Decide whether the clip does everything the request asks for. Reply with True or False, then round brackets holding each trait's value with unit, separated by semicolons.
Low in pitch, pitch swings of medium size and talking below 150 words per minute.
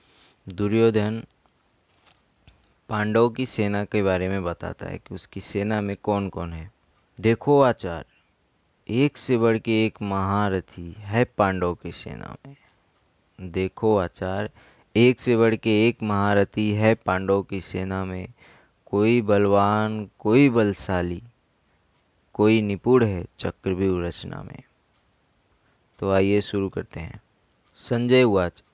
True (100 Hz; 3.2 semitones; 125 wpm)